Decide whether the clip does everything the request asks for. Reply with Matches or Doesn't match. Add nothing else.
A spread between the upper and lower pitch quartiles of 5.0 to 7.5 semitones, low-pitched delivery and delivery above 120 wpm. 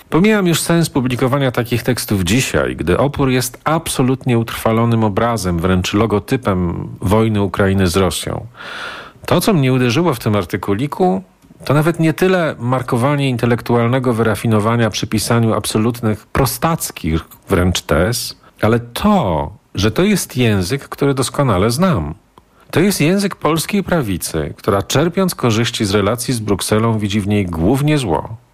Matches